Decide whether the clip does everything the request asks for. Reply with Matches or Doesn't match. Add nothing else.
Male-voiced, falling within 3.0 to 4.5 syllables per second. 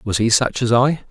Doesn't match